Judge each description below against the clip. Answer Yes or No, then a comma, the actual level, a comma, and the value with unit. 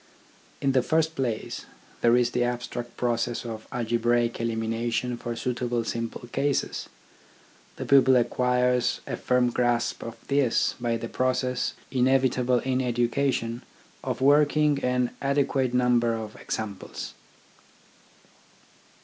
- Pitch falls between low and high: No, low, 125 Hz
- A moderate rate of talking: No, slow, 115 wpm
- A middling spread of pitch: No, narrow, 1.7 semitones